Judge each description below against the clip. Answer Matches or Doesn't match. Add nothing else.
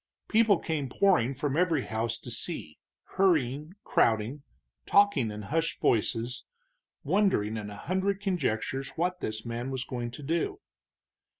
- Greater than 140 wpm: Doesn't match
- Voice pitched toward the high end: Doesn't match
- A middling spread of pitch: Doesn't match